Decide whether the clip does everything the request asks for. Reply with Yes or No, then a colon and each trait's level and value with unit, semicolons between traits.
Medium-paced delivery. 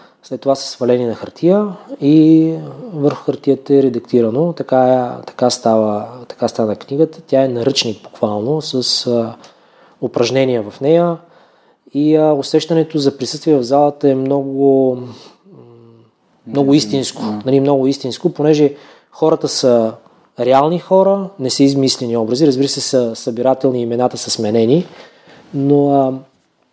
Yes: average, 130 wpm